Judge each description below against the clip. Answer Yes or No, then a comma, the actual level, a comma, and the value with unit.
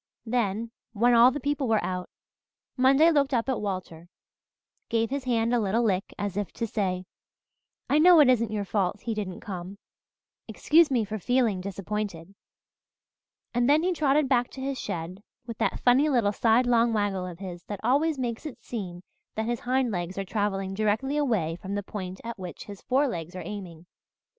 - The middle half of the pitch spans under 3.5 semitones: No, average, 4.8 semitones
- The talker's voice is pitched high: Yes, high, 220 Hz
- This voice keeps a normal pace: Yes, average, 180 wpm